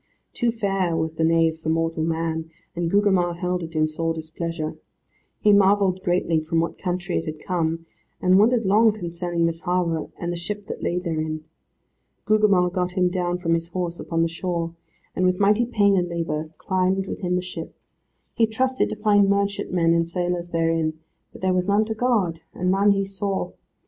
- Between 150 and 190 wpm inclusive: Yes, average, 185 wpm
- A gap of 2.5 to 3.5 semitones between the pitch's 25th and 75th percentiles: Yes, average, 3.0 semitones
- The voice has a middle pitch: Yes, medium, 180 Hz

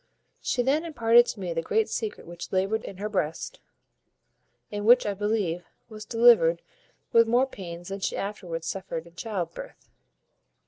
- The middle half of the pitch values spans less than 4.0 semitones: No, average, 4.9 semitones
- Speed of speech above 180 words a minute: No, average, 165 wpm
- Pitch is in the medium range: No, high, 205 Hz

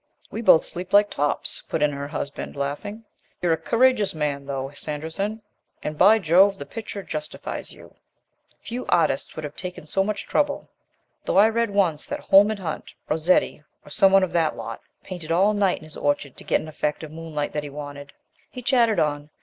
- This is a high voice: No, medium, 165 Hz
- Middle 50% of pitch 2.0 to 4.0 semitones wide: No, wide, 5.4 semitones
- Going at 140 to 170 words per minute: No, average, 195 wpm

